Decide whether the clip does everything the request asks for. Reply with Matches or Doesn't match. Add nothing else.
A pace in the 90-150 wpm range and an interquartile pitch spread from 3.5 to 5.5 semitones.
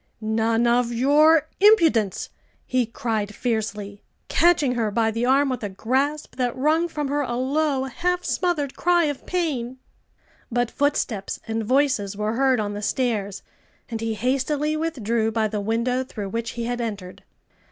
Doesn't match